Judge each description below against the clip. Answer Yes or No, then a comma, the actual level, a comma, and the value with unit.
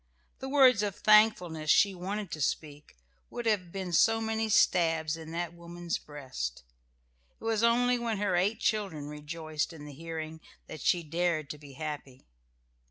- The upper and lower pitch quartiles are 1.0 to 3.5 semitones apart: No, wide, 5.6 semitones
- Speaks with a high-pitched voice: No, medium, 170 Hz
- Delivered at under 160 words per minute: No, average, 165 wpm